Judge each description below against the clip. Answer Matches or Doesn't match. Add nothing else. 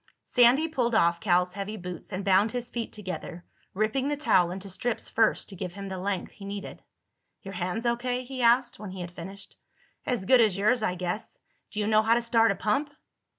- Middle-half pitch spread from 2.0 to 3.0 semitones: Doesn't match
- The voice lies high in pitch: Matches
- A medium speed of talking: Doesn't match